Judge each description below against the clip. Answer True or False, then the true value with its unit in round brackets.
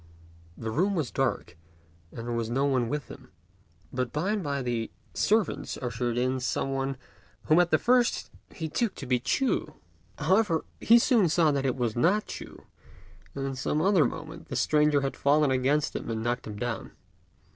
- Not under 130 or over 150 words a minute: False (180 wpm)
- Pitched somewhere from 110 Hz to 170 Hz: True (140 Hz)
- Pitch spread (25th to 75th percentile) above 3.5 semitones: True (5.1 semitones)